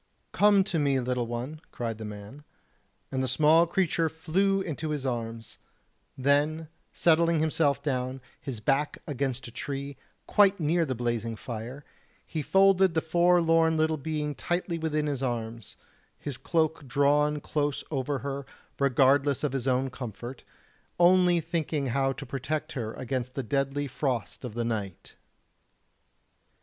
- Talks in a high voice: No, medium, 140 Hz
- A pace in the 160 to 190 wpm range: No, average, 145 wpm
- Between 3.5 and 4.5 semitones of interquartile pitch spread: Yes, average, 3.9 semitones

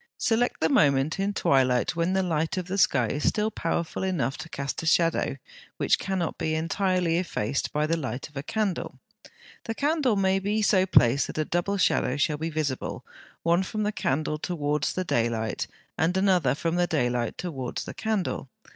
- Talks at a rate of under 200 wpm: Yes, average, 185 wpm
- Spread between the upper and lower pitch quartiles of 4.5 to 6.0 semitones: Yes, average, 5.2 semitones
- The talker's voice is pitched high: No, medium, 165 Hz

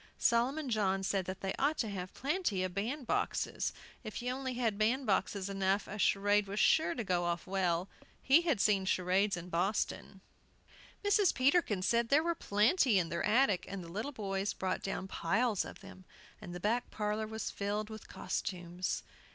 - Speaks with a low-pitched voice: No, high, 205 Hz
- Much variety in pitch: No, average, 4.3 semitones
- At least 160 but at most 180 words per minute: Yes, average, 175 wpm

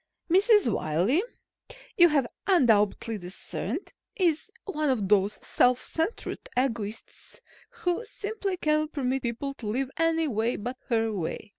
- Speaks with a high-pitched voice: Yes, very high, 265 Hz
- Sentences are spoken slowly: Yes, slow, 130 wpm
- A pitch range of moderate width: No, wide, 6.8 semitones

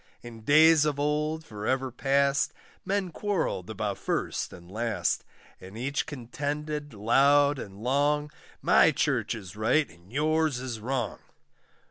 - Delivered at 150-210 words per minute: No, slow, 135 wpm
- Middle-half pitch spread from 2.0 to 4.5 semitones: No, average, 5.0 semitones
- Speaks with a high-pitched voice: No, medium, 140 Hz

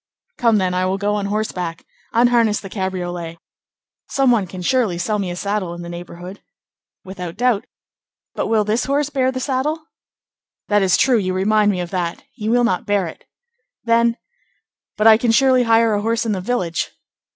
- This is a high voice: Yes, high, 210 Hz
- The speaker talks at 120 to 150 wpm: No, average, 185 wpm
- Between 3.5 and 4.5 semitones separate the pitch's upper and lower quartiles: Yes, average, 4.1 semitones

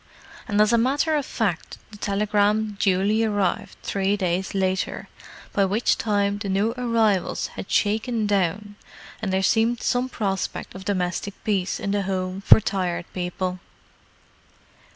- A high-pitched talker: Yes, high, 205 Hz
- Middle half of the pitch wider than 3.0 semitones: No, narrow, 2.4 semitones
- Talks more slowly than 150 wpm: Yes, average, 140 wpm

